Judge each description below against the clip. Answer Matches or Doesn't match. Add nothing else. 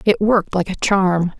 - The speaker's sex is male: Doesn't match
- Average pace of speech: Doesn't match